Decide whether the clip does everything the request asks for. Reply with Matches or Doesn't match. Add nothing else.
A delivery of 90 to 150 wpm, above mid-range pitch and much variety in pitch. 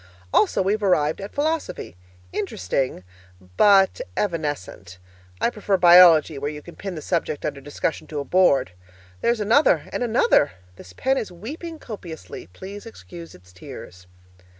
Doesn't match